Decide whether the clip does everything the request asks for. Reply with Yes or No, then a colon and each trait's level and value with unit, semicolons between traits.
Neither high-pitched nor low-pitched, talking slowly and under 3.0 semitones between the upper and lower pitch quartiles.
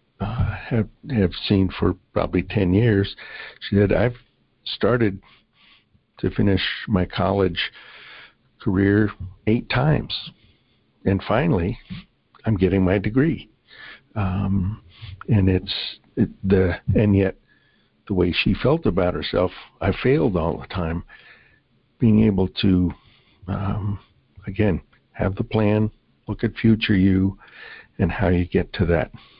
No: low, 100 Hz; slow, 125 wpm; narrow, 2.4 semitones